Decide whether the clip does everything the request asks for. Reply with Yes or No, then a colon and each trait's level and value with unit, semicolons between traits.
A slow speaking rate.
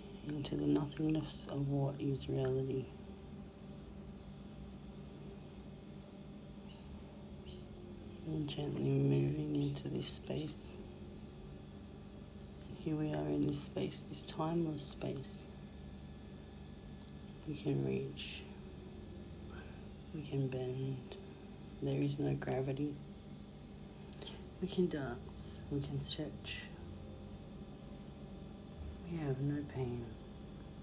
Yes: slow, 80 wpm